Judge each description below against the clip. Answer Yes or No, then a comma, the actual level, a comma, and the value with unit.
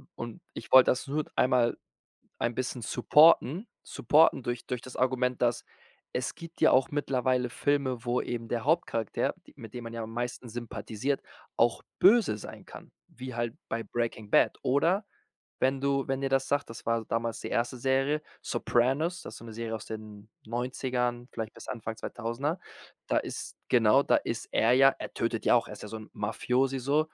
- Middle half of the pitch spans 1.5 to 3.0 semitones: Yes, average, 2.7 semitones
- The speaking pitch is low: Yes, low, 125 Hz